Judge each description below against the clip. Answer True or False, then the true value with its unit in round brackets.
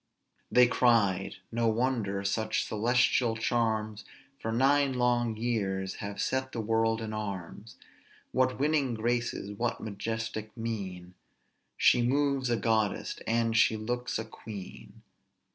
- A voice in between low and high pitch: False (115 Hz)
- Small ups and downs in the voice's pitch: True (2.3 semitones)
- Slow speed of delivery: True (125 wpm)